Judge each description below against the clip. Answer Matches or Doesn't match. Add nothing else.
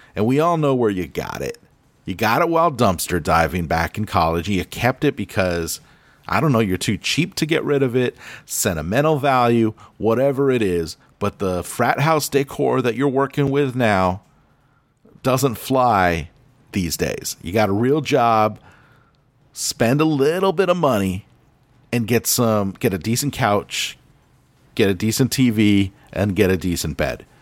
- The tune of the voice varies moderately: Doesn't match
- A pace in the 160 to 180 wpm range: Matches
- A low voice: Matches